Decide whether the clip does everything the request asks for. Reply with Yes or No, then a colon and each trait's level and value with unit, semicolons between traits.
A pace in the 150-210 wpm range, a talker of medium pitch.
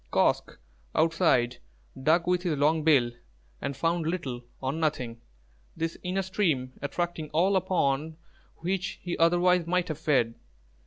No: slow, 135 wpm; medium, 165 Hz